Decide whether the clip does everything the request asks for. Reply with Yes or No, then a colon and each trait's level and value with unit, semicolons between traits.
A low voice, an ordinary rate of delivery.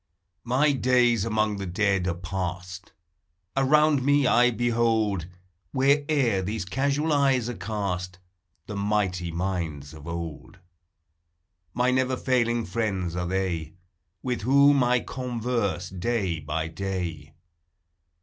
No: low, 105 Hz; slow, 115 wpm